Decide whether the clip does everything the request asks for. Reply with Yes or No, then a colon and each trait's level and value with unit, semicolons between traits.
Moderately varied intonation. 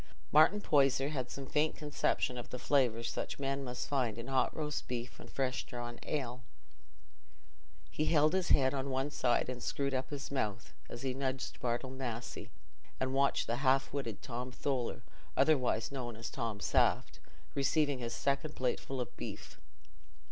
No: narrow, 2.3 semitones